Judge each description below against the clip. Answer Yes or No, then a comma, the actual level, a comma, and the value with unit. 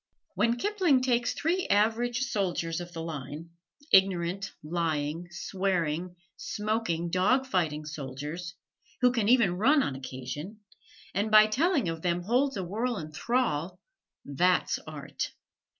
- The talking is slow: Yes, slow, 130 wpm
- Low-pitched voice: No, medium, 185 Hz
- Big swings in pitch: Yes, wide, 6.2 semitones